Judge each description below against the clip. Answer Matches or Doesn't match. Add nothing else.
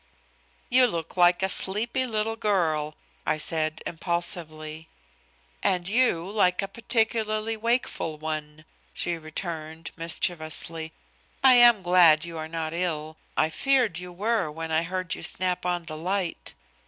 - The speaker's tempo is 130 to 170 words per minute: Matches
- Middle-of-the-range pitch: Matches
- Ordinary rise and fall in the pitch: Matches